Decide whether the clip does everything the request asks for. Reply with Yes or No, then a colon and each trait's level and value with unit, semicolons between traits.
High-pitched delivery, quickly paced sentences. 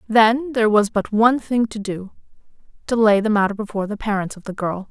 Yes: high, 215 Hz; fast, 210 wpm